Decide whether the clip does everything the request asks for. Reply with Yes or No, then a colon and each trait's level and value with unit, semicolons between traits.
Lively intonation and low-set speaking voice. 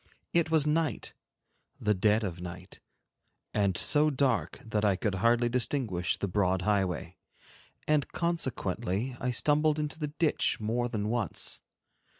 Yes: wide, 7.2 semitones; low, 115 Hz